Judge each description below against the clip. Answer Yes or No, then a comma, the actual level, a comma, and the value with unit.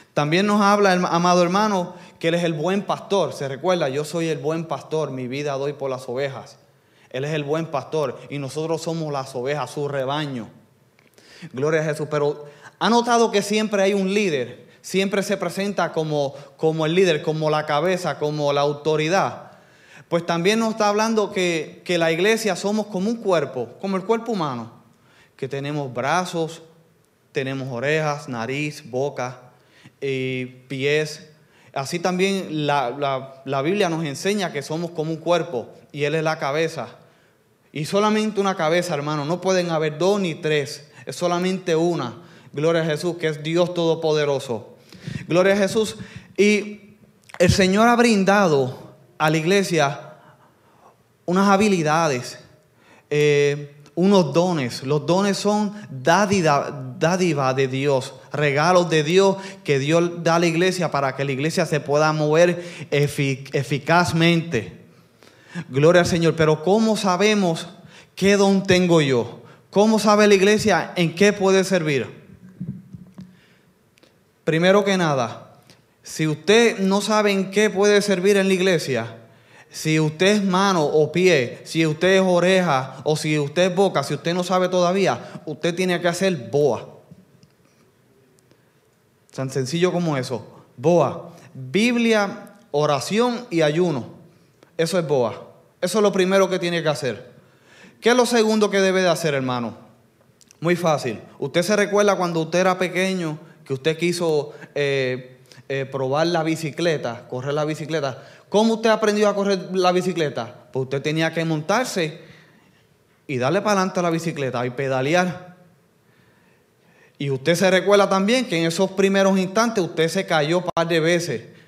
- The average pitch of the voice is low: No, medium, 165 Hz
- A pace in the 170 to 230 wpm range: No, average, 155 wpm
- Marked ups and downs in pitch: No, average, 4.6 semitones